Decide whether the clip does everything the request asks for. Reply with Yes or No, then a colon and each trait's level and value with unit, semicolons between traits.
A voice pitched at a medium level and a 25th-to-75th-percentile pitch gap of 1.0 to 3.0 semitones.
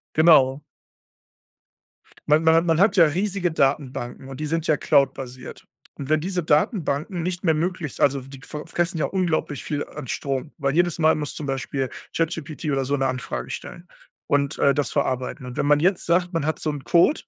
No: medium, 150 Hz; average, 3.4 semitones